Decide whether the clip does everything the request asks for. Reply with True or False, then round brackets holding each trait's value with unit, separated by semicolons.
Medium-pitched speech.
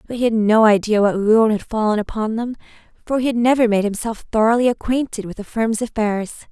False (220 Hz)